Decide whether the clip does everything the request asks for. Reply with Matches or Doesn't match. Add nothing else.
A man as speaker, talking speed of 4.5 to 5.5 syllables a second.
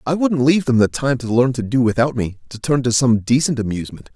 Doesn't match